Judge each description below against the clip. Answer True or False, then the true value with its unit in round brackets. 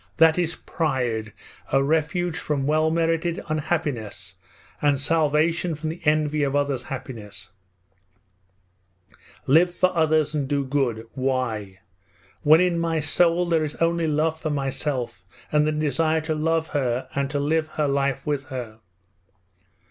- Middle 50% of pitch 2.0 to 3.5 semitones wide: True (3.1 semitones)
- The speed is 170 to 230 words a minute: False (140 wpm)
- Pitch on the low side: False (150 Hz)